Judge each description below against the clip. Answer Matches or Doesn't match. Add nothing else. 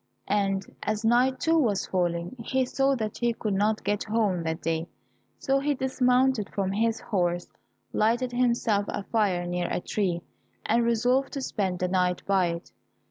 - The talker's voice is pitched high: Matches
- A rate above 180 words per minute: Doesn't match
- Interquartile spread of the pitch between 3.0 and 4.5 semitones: Doesn't match